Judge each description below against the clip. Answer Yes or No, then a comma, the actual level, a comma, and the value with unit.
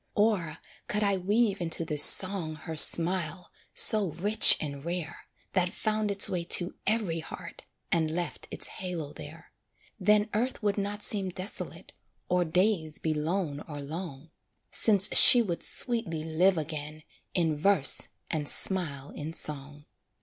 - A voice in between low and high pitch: Yes, medium, 175 Hz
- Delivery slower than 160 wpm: Yes, average, 145 wpm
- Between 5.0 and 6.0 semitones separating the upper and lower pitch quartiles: No, average, 4.3 semitones